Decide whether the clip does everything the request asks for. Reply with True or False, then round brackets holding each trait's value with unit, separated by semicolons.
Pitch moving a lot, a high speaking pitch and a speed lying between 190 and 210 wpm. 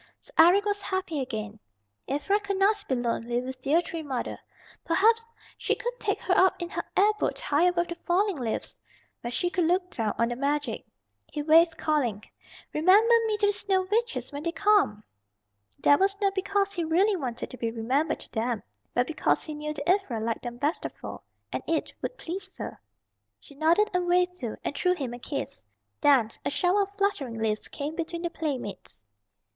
True (6.9 semitones; 325 Hz; 195 wpm)